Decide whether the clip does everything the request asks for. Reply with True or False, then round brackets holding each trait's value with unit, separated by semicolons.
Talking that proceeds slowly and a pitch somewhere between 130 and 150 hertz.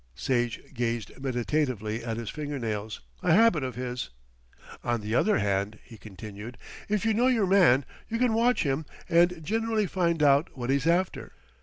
False (170 wpm; 135 Hz)